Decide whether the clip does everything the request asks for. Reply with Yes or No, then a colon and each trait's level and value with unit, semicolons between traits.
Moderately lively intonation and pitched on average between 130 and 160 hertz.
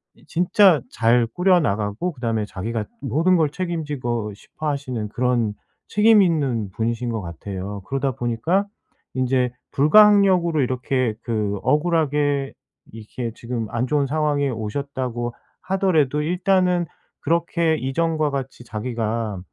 No: wide, 5.9 semitones; low, 135 Hz